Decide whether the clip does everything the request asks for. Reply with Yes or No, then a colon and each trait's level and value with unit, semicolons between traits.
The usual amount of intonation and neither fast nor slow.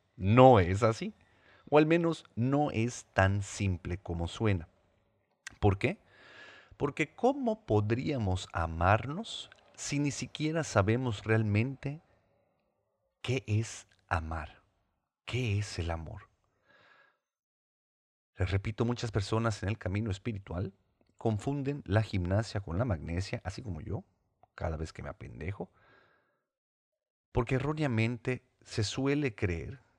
No: average, 4.7 semitones; slow, 115 wpm